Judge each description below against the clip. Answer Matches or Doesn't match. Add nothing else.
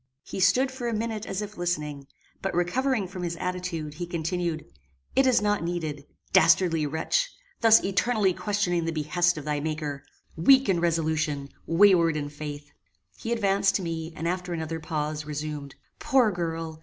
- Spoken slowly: Doesn't match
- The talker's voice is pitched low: Doesn't match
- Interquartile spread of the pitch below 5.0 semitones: Matches